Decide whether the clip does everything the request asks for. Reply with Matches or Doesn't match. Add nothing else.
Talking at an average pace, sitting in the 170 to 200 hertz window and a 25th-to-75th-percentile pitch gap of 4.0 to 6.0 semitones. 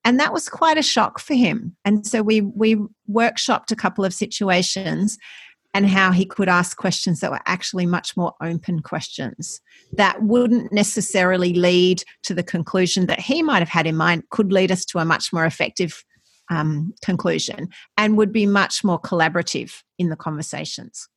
Doesn't match